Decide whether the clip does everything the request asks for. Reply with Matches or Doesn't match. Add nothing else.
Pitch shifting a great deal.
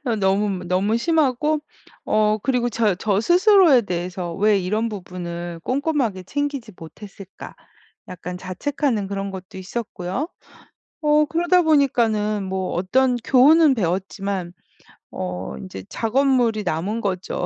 Matches